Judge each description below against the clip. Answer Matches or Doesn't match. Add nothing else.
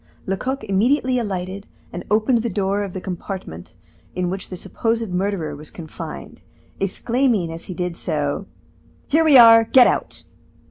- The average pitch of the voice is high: Matches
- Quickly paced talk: Doesn't match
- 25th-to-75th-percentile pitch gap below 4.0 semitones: Doesn't match